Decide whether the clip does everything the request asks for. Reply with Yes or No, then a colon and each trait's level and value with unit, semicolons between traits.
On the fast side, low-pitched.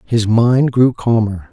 No: average, 160 wpm; low, 115 Hz